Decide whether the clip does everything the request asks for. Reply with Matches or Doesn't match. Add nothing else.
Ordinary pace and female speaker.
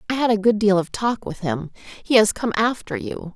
Doesn't match